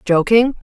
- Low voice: No, high, 215 Hz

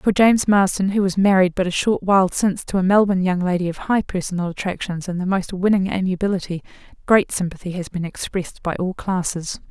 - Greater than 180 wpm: Yes, fast, 205 wpm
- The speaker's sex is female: Yes, female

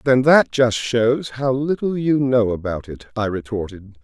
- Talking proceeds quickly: No, average, 180 wpm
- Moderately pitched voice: No, low, 120 Hz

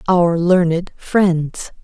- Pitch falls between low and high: Yes, medium, 175 Hz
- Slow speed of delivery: Yes, slow, 100 wpm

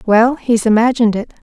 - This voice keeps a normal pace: Yes, average, 160 wpm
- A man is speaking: No, female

